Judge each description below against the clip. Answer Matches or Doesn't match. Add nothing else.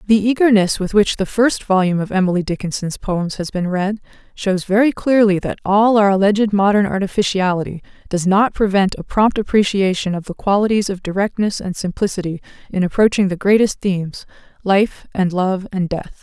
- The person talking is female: Matches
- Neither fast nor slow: Matches